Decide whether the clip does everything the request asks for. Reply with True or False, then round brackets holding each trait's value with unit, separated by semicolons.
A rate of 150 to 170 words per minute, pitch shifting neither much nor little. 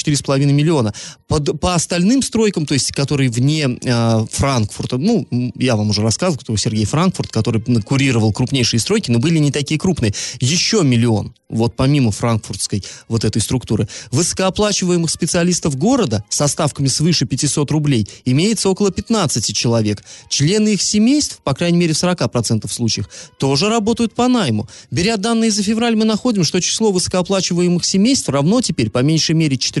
False (155 wpm; 7.4 semitones)